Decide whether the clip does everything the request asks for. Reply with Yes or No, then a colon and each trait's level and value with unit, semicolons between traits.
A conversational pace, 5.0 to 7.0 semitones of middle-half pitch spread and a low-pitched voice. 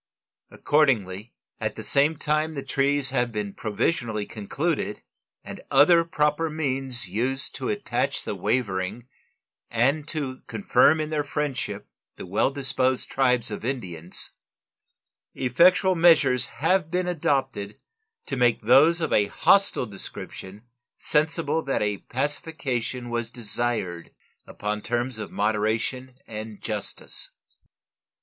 No: slow, 120 wpm; wide, 5.5 semitones; low, 130 Hz